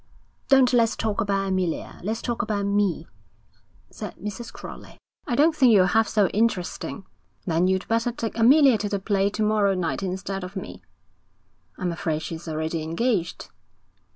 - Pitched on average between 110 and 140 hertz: No, high, 200 Hz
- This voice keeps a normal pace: Yes, average, 160 wpm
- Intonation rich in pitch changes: No, average, 3.7 semitones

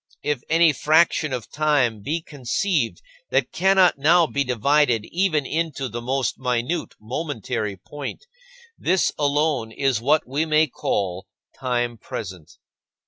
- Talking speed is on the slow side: Yes, slow, 130 wpm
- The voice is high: No, medium, 140 Hz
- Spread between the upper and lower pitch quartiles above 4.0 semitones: Yes, average, 4.7 semitones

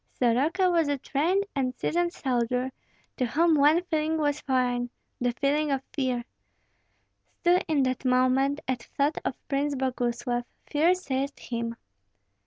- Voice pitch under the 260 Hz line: No, very high, 275 Hz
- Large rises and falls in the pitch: No, average, 3.3 semitones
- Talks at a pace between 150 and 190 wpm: No, average, 140 wpm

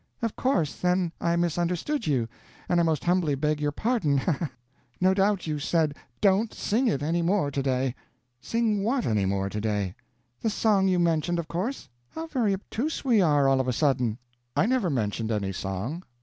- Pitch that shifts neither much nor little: No, wide, 6.8 semitones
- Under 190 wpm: No, average, 195 wpm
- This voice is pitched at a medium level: Yes, medium, 170 Hz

